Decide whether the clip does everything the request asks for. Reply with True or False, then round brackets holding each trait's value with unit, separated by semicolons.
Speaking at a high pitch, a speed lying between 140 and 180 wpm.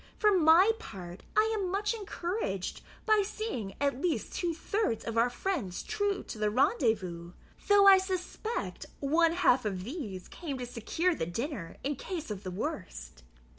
True (290 Hz; 165 wpm)